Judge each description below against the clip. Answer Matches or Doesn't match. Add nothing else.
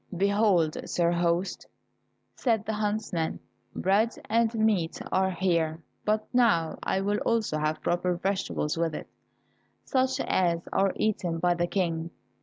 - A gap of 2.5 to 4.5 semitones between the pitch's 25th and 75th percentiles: Matches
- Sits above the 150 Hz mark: Matches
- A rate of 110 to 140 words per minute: Matches